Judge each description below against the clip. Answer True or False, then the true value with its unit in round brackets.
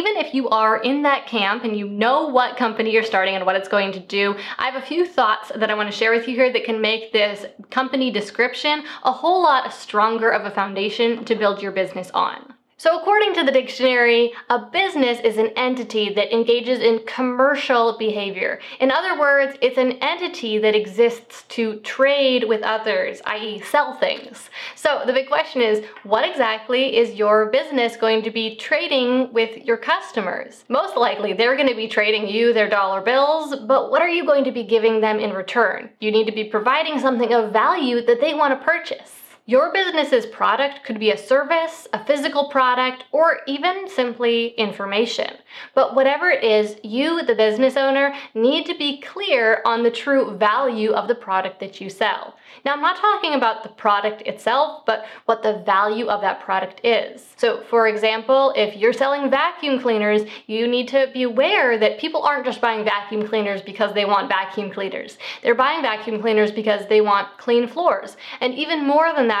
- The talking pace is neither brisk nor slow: True (195 wpm)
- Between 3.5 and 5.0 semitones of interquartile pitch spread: True (4.2 semitones)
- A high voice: True (235 Hz)